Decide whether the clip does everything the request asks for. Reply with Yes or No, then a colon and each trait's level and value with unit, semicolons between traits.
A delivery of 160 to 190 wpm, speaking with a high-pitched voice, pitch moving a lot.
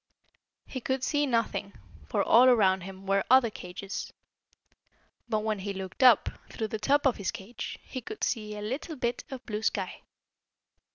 No: average, 170 wpm; high, 220 Hz; average, 4.4 semitones